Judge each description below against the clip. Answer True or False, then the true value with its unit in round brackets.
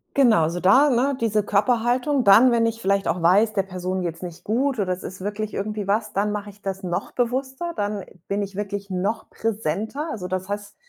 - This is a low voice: False (205 Hz)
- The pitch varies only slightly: False (3.2 semitones)